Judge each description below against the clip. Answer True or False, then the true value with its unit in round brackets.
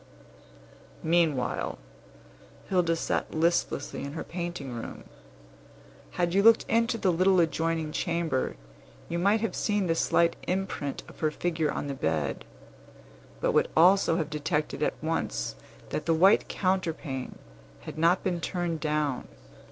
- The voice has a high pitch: False (165 Hz)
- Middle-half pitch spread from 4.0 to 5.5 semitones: False (3.0 semitones)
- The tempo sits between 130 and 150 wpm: True (135 wpm)